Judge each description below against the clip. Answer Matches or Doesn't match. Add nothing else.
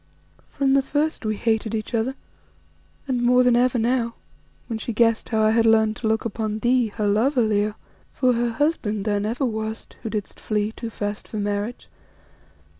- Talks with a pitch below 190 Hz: Doesn't match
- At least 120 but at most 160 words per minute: Doesn't match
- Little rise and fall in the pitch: Matches